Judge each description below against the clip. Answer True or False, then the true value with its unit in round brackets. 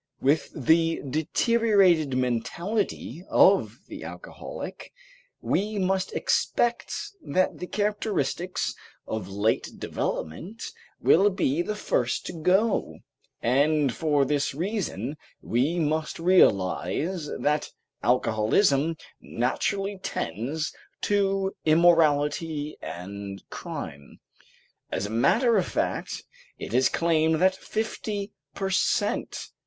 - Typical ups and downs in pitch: False (6.3 semitones)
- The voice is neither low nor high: True (160 Hz)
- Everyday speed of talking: False (100 wpm)